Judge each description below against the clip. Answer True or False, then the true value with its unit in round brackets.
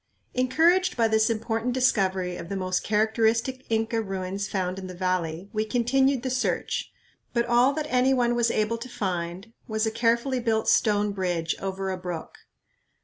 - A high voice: True (220 Hz)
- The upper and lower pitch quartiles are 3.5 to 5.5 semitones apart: True (4.3 semitones)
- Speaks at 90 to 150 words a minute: False (170 wpm)